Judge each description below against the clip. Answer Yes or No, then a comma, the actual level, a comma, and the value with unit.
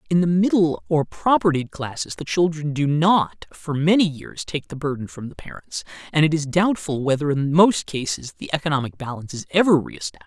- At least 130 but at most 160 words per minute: No, average, 195 wpm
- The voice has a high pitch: No, medium, 155 Hz